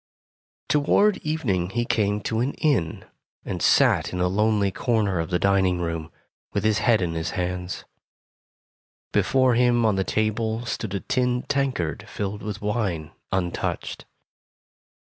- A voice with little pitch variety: No, average, 4.6 semitones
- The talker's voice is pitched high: No, low, 105 Hz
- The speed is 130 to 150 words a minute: Yes, average, 145 wpm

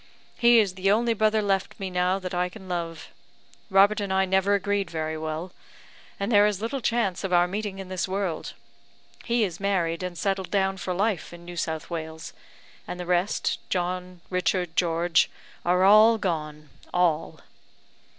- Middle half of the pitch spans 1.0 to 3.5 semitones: Yes, narrow, 2.5 semitones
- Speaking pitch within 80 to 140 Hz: No, medium, 185 Hz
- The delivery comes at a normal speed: Yes, average, 170 wpm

